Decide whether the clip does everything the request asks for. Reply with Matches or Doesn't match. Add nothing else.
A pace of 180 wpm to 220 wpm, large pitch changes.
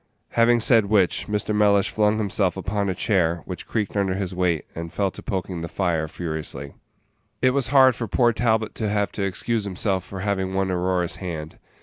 Doesn't match